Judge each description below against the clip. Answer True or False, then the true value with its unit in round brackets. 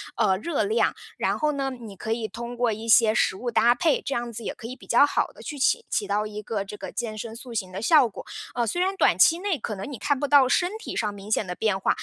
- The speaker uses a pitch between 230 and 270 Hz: True (235 Hz)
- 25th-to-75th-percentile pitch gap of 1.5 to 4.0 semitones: False (4.9 semitones)